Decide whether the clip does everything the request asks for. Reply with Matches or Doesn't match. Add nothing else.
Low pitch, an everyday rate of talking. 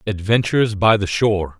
Matches